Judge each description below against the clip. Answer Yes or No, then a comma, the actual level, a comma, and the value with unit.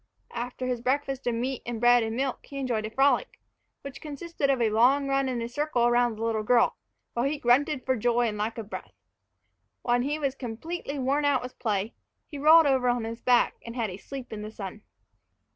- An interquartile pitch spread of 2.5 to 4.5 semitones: Yes, average, 3.1 semitones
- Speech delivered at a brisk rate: Yes, fast, 215 wpm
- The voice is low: No, high, 245 Hz